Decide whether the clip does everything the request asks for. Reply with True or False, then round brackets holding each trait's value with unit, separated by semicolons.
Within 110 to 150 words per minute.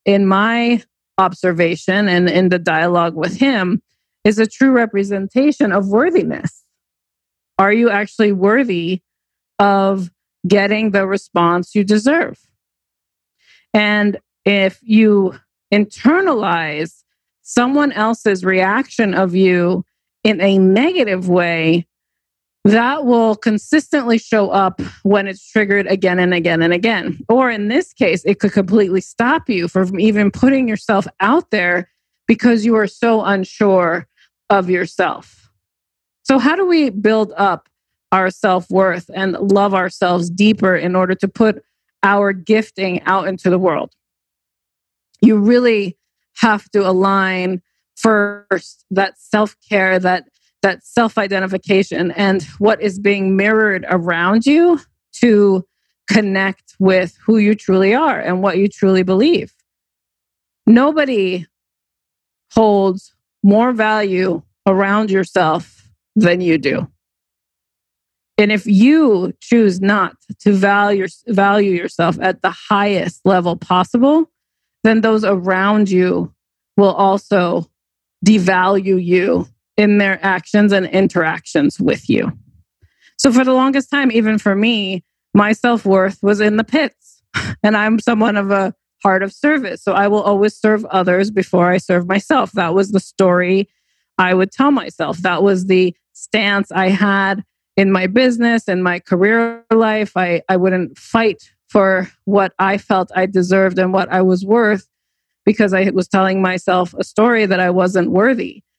True (135 wpm)